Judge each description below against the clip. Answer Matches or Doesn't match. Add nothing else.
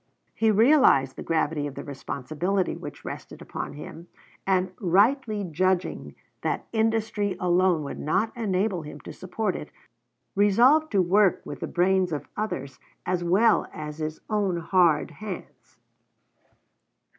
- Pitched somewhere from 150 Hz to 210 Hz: Matches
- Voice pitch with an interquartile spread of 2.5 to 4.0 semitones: Doesn't match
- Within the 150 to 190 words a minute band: Doesn't match